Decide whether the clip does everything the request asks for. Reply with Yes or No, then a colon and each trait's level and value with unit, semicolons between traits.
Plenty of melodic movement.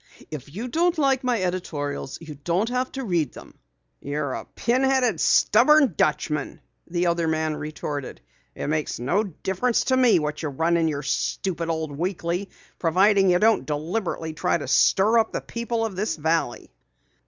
Yes: wide, 6.7 semitones